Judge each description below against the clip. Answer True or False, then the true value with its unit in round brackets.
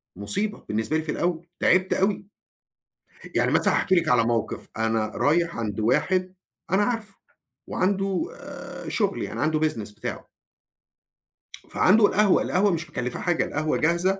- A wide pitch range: True (8.0 semitones)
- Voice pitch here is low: False (170 Hz)